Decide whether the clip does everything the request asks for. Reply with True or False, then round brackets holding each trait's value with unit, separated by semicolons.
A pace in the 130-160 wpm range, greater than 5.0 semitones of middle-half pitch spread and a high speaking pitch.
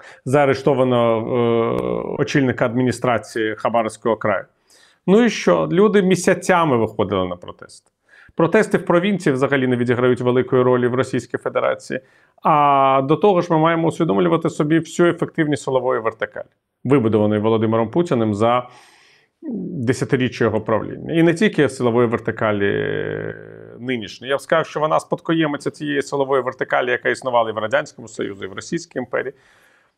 False (140 wpm; 5.5 semitones; 135 Hz)